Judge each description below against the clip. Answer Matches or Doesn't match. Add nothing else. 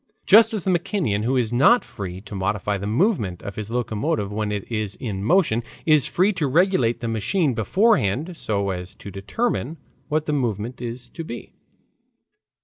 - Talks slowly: Doesn't match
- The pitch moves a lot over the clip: Matches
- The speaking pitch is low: Matches